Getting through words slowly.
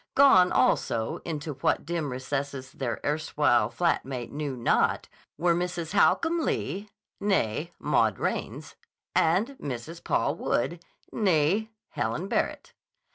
Yes: slow, 120 wpm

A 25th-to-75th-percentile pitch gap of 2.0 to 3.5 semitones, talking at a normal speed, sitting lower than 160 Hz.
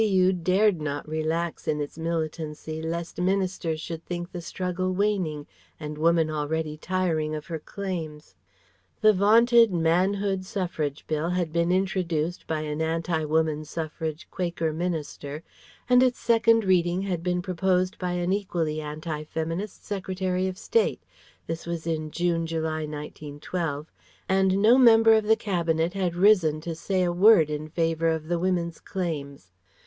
No: average, 3.0 semitones; average, 150 wpm; medium, 170 Hz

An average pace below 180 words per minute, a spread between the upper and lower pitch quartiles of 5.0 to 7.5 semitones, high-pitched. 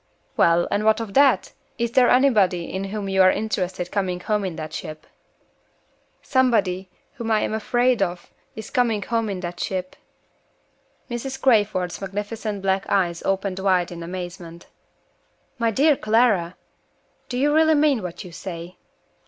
No: average, 155 wpm; average, 4.3 semitones; high, 200 Hz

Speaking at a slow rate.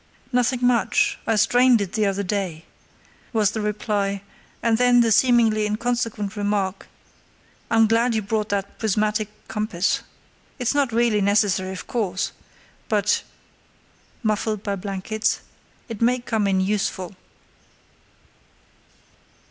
Yes: slow, 120 wpm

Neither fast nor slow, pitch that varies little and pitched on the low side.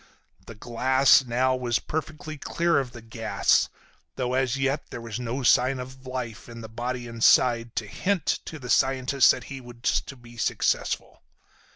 Yes: average, 170 wpm; narrow, 2.2 semitones; low, 125 Hz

